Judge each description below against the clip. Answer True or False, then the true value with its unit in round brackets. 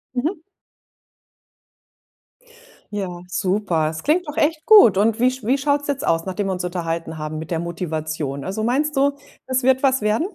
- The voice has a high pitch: True (210 Hz)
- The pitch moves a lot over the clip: True (8.3 semitones)